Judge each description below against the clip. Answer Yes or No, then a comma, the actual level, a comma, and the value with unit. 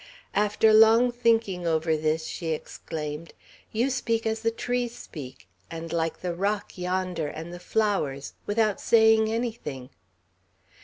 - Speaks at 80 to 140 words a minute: Yes, slow, 135 wpm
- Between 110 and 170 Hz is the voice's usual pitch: No, high, 195 Hz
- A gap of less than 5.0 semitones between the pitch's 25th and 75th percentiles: No, wide, 5.5 semitones